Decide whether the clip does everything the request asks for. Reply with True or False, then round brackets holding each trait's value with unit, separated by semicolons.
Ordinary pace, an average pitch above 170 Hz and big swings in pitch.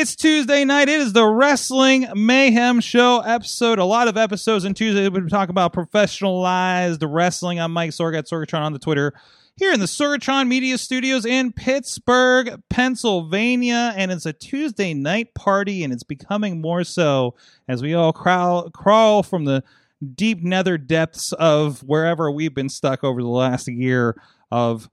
True (165 wpm; 190 Hz; 7.1 semitones)